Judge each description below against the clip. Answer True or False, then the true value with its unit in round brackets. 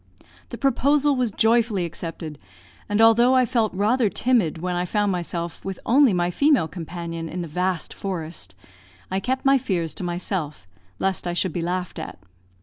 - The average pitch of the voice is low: False (185 Hz)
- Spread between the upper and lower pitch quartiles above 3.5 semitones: True (5.5 semitones)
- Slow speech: False (170 wpm)